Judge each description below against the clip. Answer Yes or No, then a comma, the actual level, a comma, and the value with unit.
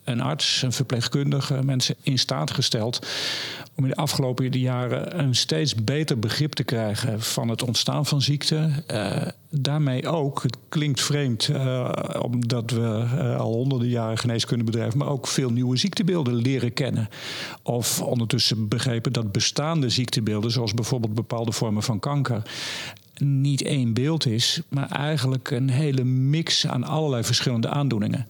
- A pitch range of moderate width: Yes, average, 3.3 semitones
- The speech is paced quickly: No, average, 150 wpm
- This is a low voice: Yes, low, 130 Hz